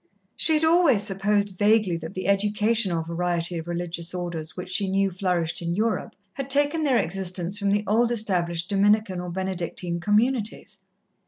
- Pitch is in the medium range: No, high, 195 Hz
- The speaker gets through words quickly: No, average, 160 wpm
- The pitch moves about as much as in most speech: Yes, average, 3.6 semitones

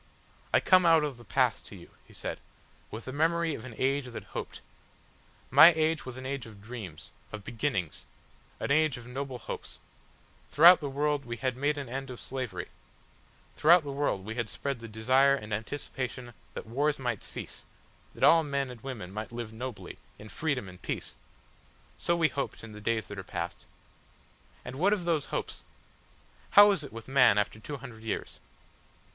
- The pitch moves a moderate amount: Yes, average, 4.5 semitones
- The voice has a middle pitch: No, low, 130 Hz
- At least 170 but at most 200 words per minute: Yes, average, 185 wpm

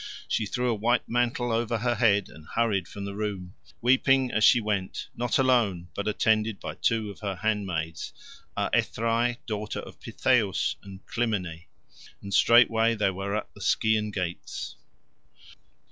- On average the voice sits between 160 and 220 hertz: No, low, 110 Hz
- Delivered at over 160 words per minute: No, average, 150 wpm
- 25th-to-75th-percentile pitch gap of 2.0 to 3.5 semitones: Yes, average, 3.0 semitones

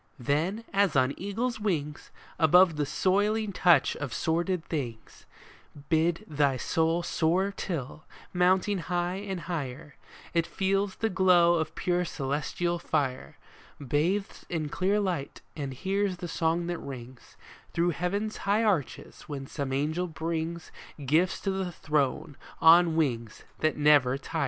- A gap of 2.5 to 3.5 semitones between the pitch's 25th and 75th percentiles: No, average, 4.1 semitones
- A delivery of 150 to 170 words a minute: No, slow, 135 wpm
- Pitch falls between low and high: Yes, medium, 170 Hz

